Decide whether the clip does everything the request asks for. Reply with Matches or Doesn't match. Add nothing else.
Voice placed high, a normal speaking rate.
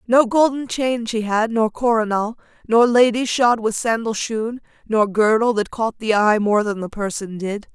Matches